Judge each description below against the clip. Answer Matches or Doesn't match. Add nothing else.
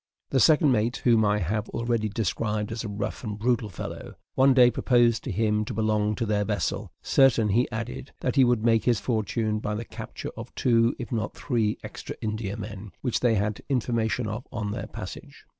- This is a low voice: Matches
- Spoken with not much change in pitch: Matches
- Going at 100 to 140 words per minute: Doesn't match